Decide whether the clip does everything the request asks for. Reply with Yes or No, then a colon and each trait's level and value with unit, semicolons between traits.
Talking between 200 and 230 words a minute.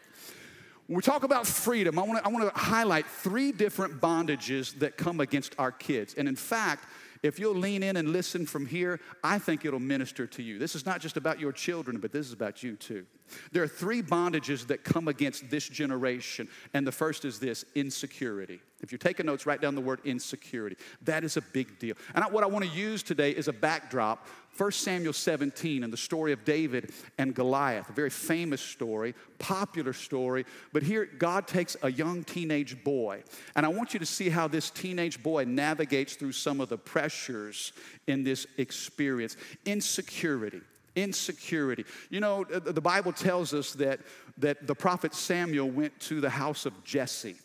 No: average, 190 wpm